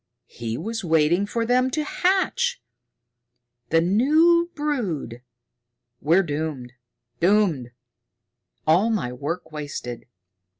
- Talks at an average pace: No, slow, 95 wpm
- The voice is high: No, medium, 180 Hz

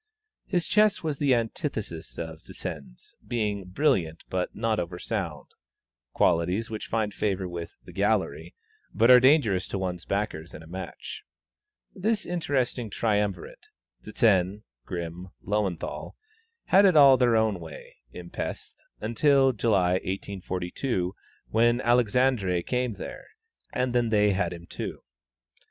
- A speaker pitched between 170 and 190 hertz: No, low, 105 Hz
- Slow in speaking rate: Yes, slow, 130 wpm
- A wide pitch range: Yes, wide, 5.7 semitones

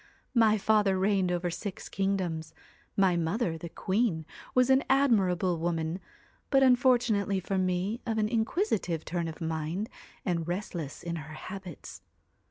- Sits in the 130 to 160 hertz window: No, high, 190 Hz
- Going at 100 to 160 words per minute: Yes, average, 150 wpm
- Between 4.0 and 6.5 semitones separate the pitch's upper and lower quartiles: Yes, average, 4.4 semitones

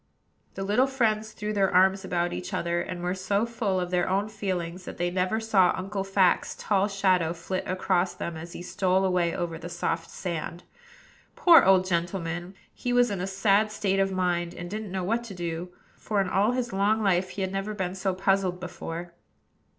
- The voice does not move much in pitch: Yes, narrow, 2.3 semitones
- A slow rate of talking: No, average, 200 wpm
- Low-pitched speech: No, high, 190 Hz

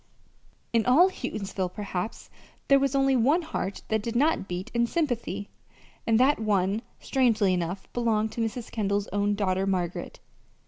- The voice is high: Yes, high, 220 Hz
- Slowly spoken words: No, average, 150 wpm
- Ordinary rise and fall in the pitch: Yes, average, 4.2 semitones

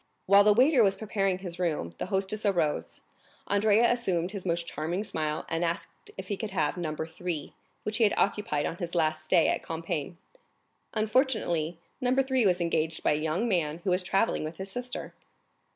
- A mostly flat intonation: No, average, 4.5 semitones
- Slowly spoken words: No, average, 185 wpm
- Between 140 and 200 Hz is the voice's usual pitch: Yes, medium, 185 Hz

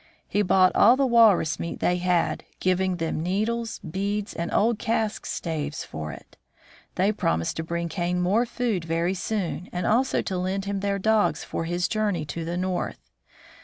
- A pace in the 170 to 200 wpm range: Yes, average, 175 wpm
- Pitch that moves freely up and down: No, average, 3.7 semitones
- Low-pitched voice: No, medium, 185 Hz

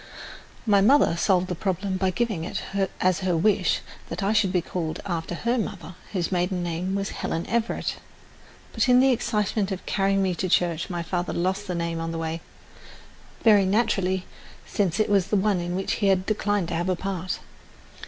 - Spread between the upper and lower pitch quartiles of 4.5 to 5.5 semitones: No, average, 2.7 semitones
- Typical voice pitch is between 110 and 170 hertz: No, high, 190 Hz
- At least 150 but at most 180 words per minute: No, average, 190 wpm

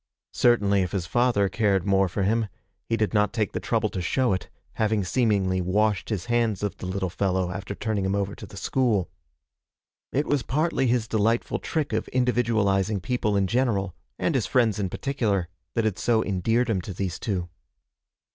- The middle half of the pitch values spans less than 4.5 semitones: Yes, average, 3.4 semitones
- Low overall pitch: Yes, low, 105 Hz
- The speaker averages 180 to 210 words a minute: Yes, average, 185 wpm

